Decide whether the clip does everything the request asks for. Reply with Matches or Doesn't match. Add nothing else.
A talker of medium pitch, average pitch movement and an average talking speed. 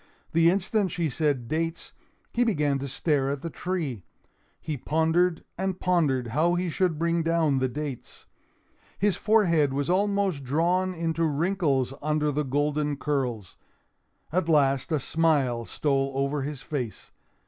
Matches